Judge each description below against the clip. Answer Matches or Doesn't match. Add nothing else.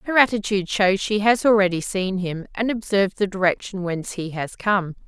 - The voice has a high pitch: Matches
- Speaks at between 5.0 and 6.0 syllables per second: Matches